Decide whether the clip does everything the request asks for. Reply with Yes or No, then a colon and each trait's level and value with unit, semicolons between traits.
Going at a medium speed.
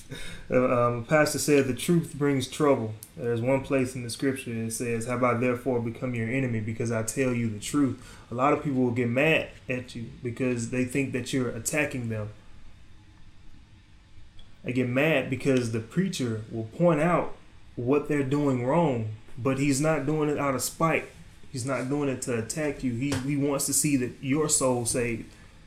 Yes: average, 190 wpm